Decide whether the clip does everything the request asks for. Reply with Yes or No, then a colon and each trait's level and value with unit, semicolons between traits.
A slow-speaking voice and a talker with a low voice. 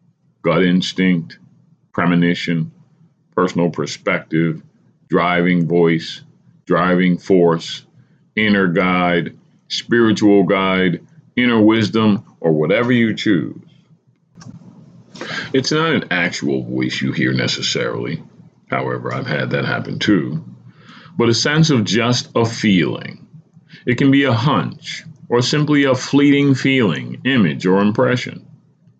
Yes: slow, 110 wpm; low, 115 Hz